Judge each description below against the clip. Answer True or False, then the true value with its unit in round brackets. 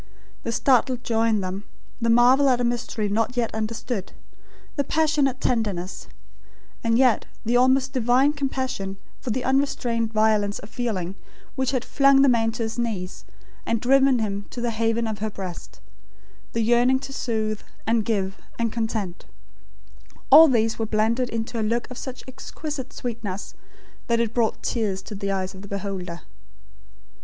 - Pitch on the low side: False (230 Hz)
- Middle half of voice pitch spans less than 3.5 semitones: True (3.0 semitones)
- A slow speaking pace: False (165 wpm)